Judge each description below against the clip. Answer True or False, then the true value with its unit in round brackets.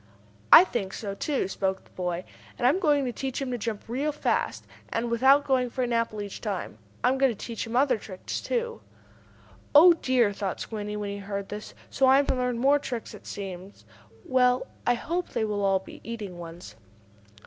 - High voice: True (235 Hz)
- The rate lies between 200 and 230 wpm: True (205 wpm)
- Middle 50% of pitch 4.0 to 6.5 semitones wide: True (4.7 semitones)